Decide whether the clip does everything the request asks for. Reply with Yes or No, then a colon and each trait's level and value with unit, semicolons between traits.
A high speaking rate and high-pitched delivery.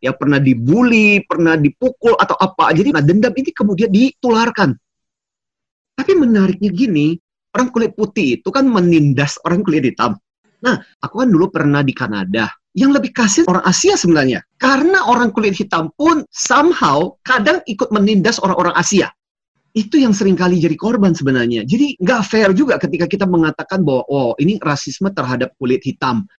Yes: fast, 155 wpm; high, 195 Hz